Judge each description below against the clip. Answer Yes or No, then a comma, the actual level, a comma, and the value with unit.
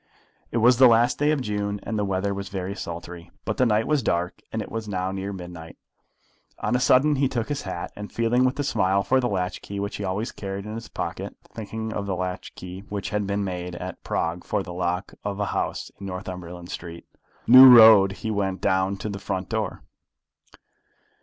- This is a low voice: Yes, low, 100 Hz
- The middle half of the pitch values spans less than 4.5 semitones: Yes, average, 3.4 semitones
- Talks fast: Yes, fast, 215 wpm